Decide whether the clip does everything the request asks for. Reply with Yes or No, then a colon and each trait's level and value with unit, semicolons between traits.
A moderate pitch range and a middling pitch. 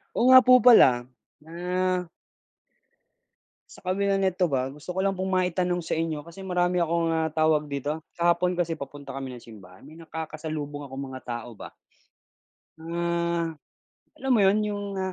Yes: average, 3.7 semitones; medium, 170 Hz